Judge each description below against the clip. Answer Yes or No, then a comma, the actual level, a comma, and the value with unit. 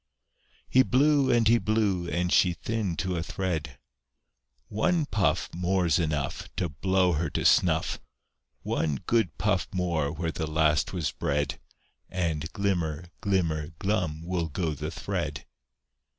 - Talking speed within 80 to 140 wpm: Yes, slow, 135 wpm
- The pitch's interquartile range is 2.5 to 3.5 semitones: No, average, 4.0 semitones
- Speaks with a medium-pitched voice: No, very low, 90 Hz